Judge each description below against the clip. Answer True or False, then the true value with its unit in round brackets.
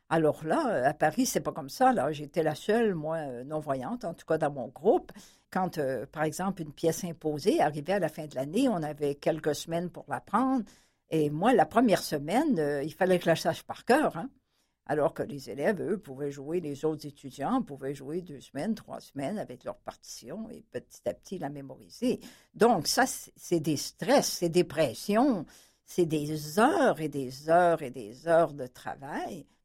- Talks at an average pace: True (200 wpm)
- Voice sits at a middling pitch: True (160 Hz)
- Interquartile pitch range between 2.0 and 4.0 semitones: False (5.0 semitones)